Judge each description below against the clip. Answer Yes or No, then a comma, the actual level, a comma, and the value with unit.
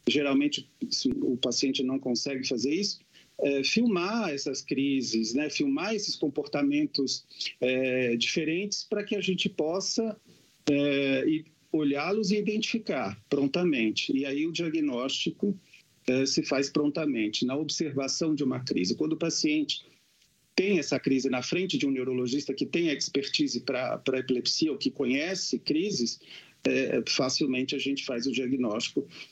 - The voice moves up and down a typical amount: No, wide, 6.1 semitones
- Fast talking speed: No, average, 145 wpm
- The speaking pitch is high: No, medium, 145 Hz